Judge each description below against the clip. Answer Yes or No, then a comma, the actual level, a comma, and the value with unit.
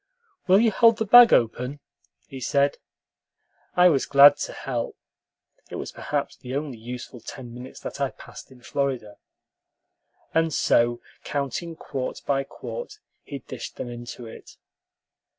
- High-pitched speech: No, low, 135 Hz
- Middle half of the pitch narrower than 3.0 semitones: No, average, 4.8 semitones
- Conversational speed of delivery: Yes, average, 145 wpm